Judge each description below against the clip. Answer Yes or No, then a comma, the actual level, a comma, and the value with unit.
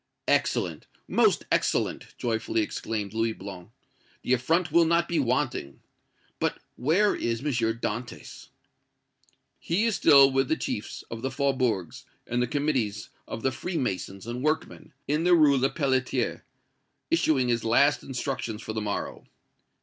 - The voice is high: No, low, 130 Hz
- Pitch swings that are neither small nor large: Yes, average, 4.8 semitones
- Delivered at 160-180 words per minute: No, average, 140 wpm